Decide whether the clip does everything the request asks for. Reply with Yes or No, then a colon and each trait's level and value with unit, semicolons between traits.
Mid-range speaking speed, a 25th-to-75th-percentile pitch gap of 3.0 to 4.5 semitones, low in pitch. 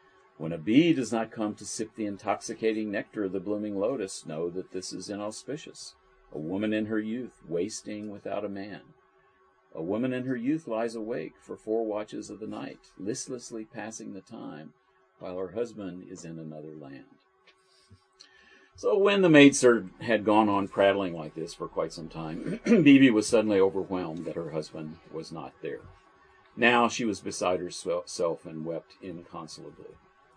Yes: average, 170 wpm; average, 3.6 semitones; low, 105 Hz